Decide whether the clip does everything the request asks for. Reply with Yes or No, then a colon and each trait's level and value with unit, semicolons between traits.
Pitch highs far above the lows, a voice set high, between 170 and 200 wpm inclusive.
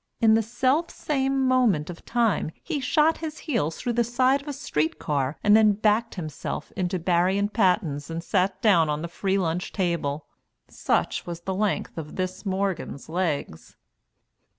Yes: wide, 6.1 semitones; high, 195 Hz; average, 175 wpm